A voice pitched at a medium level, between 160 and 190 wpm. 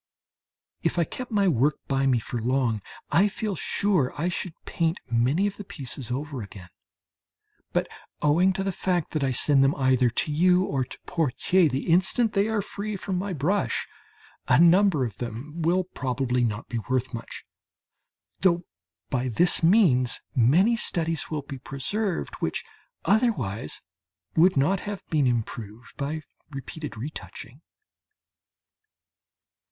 No: medium, 150 Hz; average, 145 wpm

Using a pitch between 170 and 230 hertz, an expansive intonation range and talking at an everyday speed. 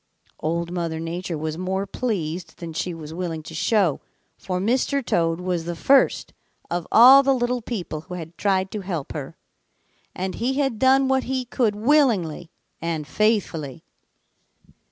Yes: medium, 185 Hz; wide, 6.3 semitones; average, 155 wpm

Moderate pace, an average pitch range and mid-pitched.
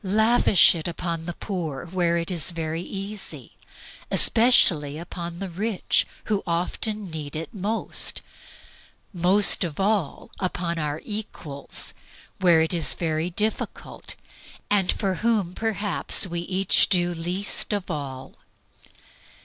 No: slow, 125 wpm; average, 3.4 semitones; medium, 180 Hz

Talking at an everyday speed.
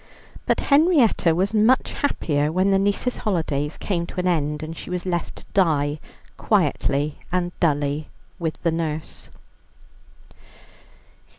No: slow, 130 wpm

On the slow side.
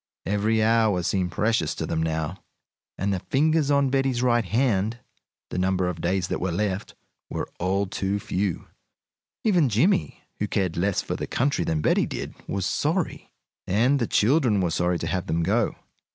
No: average, 175 wpm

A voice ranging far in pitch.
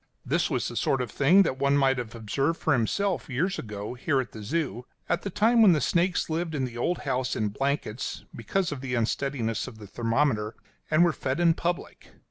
Yes: wide, 6.0 semitones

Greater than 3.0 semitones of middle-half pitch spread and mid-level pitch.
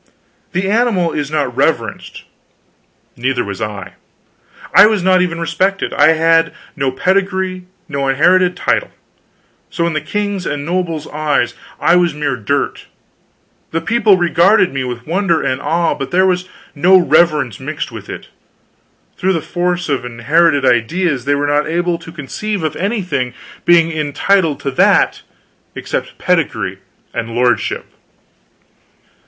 Yes: average, 4.6 semitones; medium, 165 Hz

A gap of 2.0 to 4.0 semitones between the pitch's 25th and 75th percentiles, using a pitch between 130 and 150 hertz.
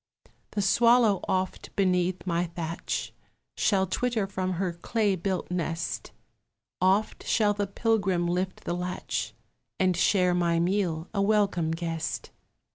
No: narrow, 2.6 semitones; medium, 185 Hz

